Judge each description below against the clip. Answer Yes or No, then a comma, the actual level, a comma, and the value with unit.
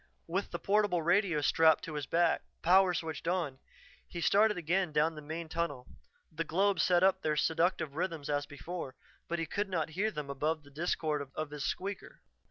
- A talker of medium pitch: Yes, medium, 165 Hz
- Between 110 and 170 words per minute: No, average, 185 wpm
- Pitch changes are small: No, average, 3.4 semitones